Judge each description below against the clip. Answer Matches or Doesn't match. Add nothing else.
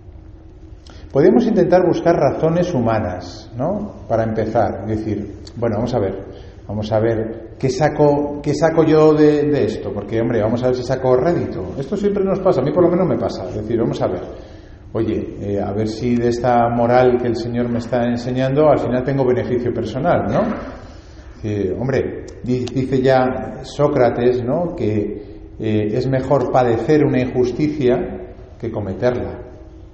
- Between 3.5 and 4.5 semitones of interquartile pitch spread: Matches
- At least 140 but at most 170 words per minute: Matches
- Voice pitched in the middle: Doesn't match